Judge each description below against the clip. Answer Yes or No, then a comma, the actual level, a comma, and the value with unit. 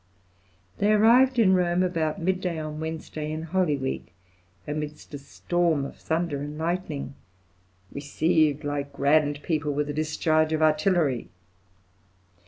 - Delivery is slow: Yes, slow, 130 wpm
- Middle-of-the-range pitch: Yes, medium, 155 Hz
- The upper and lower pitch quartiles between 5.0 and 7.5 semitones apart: No, average, 2.9 semitones